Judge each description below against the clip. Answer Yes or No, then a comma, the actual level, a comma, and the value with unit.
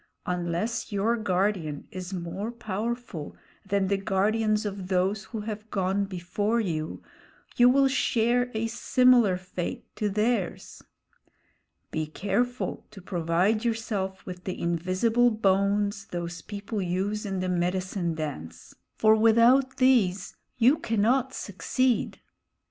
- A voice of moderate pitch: No, high, 200 Hz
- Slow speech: Yes, slow, 120 wpm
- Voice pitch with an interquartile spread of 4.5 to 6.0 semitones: No, average, 3.7 semitones